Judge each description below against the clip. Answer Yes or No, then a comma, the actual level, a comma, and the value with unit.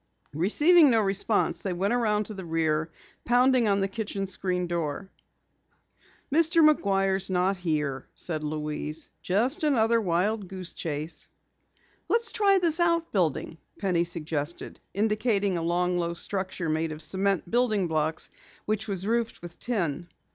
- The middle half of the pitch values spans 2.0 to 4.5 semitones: No, average, 4.9 semitones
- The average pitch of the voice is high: Yes, high, 195 Hz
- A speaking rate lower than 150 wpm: Yes, average, 140 wpm